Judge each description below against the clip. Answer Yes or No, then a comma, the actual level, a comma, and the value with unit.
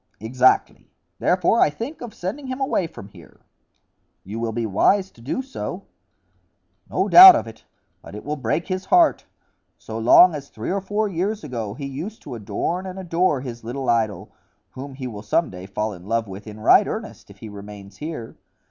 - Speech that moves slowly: No, average, 190 wpm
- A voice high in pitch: No, low, 130 Hz